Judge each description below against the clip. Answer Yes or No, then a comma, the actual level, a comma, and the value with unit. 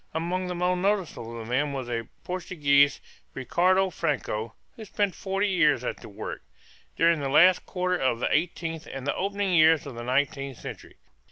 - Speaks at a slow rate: No, average, 175 wpm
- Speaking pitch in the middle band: Yes, medium, 160 Hz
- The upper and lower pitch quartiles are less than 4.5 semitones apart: No, wide, 5.4 semitones